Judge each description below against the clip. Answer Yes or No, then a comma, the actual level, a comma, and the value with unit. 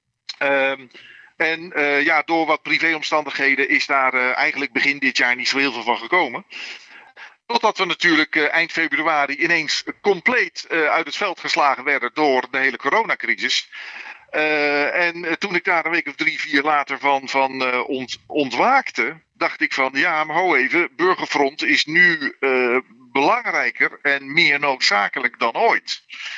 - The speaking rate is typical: Yes, average, 160 wpm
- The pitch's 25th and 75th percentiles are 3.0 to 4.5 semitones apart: Yes, average, 3.3 semitones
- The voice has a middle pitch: Yes, medium, 145 Hz